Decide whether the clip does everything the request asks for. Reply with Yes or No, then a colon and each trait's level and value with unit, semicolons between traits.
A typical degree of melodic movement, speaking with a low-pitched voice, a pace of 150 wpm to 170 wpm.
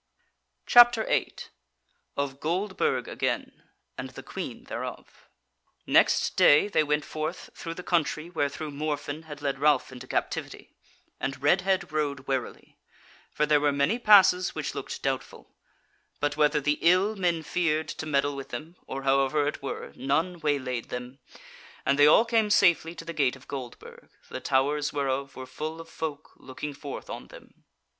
No: average, 3.1 semitones; medium, 150 Hz; average, 160 wpm